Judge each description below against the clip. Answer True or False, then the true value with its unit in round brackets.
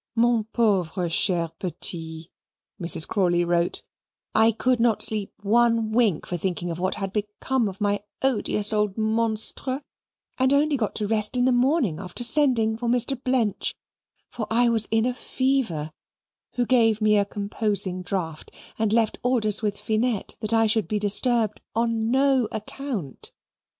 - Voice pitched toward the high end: True (220 Hz)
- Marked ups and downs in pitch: False (3.4 semitones)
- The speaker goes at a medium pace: True (155 wpm)